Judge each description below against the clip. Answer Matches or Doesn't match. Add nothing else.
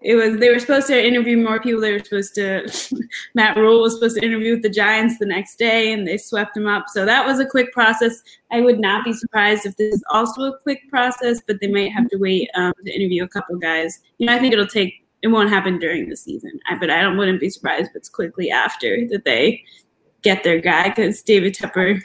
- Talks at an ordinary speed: Doesn't match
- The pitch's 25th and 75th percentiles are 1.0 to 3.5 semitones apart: Matches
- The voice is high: Matches